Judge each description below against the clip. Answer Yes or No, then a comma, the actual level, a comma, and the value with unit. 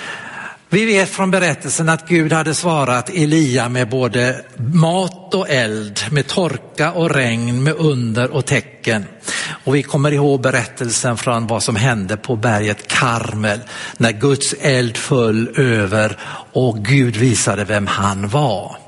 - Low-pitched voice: Yes, low, 130 Hz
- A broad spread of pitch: No, average, 5.0 semitones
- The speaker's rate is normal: Yes, average, 145 wpm